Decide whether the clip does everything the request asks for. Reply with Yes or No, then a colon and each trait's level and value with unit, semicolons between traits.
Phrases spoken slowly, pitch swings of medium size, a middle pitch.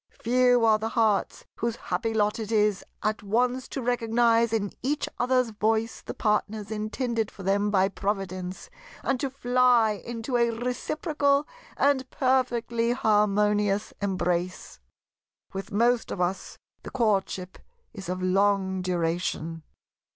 No: slow, 130 wpm; average, 3.6 semitones; high, 220 Hz